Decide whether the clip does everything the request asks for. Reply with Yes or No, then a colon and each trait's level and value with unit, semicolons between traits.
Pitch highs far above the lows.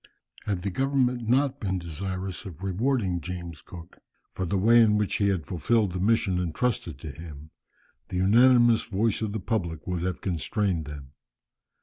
No: average, 4.5 semitones